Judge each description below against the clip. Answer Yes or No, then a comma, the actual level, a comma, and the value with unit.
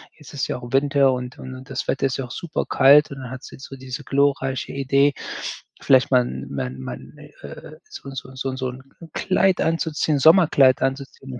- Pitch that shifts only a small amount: Yes, narrow, 1.7 semitones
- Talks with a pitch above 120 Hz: Yes, low, 135 Hz